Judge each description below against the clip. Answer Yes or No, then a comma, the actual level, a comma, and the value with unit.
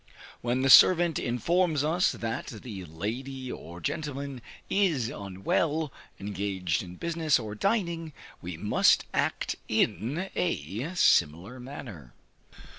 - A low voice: Yes, low, 125 Hz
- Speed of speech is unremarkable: No, slow, 115 wpm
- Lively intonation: Yes, wide, 8.1 semitones